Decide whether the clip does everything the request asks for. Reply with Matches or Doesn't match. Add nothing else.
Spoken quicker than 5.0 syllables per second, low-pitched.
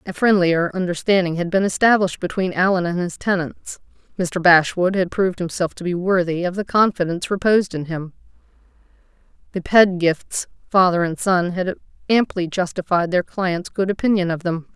Doesn't match